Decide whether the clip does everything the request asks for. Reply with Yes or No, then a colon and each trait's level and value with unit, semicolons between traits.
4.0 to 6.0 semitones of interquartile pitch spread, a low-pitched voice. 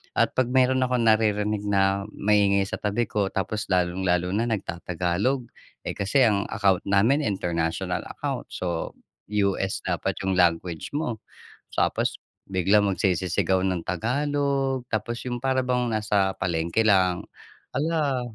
Yes: average, 4.6 semitones; low, 100 Hz